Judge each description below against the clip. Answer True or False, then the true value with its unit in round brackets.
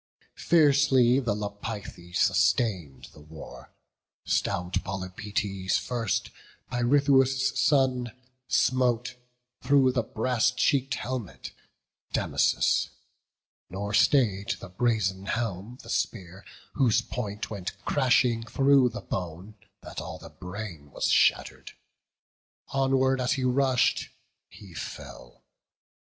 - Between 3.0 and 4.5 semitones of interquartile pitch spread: False (5.2 semitones)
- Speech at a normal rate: False (100 wpm)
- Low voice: True (115 Hz)